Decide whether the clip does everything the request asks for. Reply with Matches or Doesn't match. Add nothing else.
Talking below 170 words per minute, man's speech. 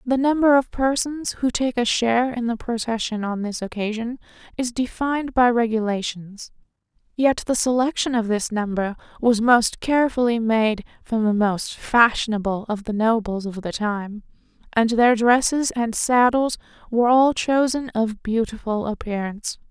Doesn't match